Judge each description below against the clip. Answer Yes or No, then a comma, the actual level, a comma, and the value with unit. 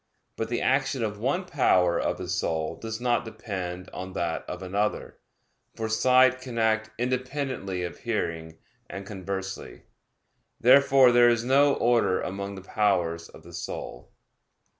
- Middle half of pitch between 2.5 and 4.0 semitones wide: No, average, 5.2 semitones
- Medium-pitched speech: No, low, 110 Hz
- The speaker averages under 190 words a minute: Yes, average, 145 wpm